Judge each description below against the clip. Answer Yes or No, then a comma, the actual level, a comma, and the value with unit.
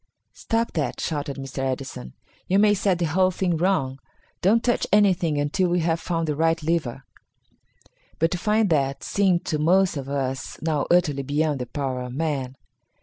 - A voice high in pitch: No, medium, 160 Hz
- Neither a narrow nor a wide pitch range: Yes, average, 4.7 semitones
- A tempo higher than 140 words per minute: Yes, average, 175 wpm